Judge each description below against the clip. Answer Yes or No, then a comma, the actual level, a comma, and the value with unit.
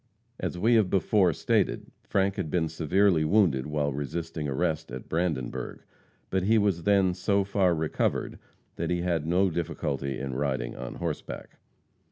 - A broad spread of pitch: No, average, 4.5 semitones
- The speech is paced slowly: No, average, 155 wpm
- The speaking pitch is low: Yes, very low, 85 Hz